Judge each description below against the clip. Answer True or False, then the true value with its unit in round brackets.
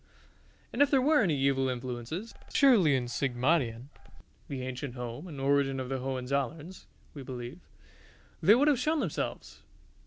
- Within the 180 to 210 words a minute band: False (150 wpm)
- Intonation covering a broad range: True (6.2 semitones)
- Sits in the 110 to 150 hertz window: True (140 Hz)